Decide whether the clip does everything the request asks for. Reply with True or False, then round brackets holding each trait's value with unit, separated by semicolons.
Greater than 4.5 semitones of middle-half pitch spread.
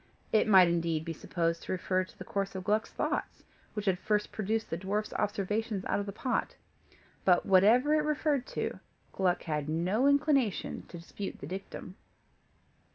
False (3.5 semitones)